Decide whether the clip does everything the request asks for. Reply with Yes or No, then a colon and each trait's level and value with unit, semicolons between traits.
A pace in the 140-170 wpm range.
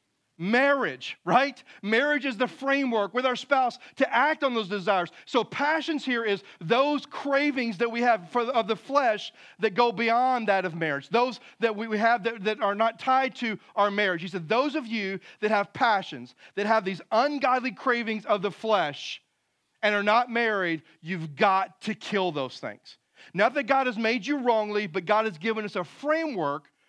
No: average, 190 wpm